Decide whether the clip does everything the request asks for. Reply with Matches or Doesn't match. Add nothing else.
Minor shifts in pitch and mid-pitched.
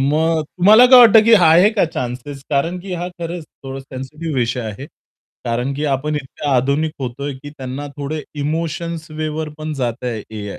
Doesn't match